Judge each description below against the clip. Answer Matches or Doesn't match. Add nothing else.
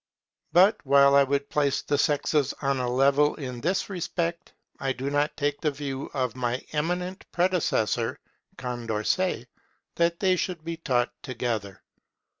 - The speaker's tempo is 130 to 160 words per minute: Matches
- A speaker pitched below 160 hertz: Matches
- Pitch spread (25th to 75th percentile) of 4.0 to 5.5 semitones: Matches